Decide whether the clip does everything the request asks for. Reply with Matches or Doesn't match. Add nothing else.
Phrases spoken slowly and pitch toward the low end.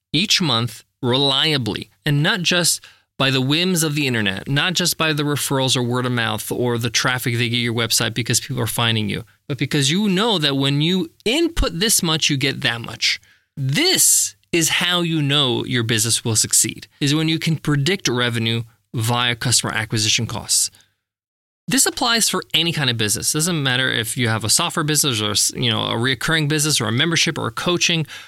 Doesn't match